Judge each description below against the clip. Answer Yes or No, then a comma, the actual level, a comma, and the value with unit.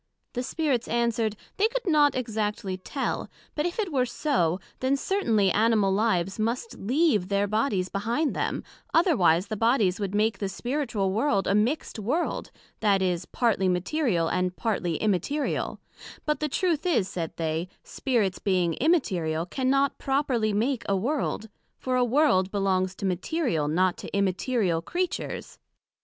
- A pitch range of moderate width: No, wide, 6.5 semitones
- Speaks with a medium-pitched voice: No, high, 220 Hz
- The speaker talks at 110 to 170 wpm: Yes, average, 150 wpm